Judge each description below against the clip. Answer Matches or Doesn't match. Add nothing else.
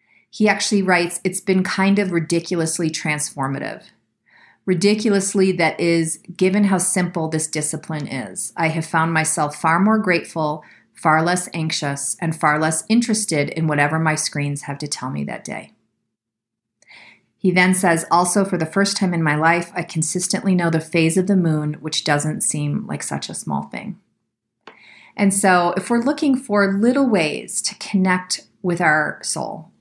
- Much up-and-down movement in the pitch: Doesn't match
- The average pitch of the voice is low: Doesn't match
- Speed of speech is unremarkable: Matches